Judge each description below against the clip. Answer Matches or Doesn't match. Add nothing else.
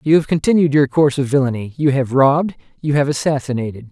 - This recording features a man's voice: Matches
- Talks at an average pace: Matches